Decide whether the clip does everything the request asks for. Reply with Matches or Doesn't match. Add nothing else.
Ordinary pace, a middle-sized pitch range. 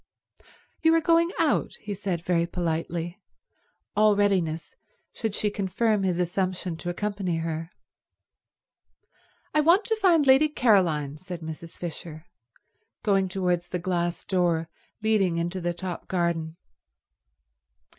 Doesn't match